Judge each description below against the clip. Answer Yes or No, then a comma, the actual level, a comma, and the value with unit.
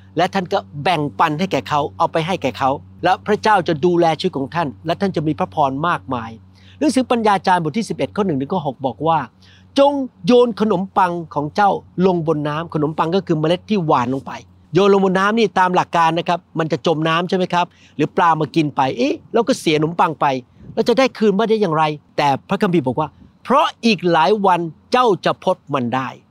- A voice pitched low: No, medium, 170 Hz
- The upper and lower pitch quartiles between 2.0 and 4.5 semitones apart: No, average, 5.0 semitones